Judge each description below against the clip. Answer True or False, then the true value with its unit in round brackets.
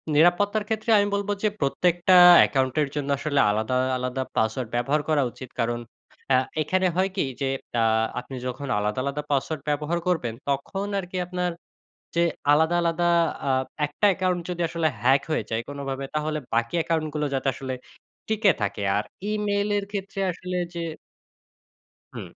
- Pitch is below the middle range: False (155 Hz)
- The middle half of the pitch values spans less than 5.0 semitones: False (5.3 semitones)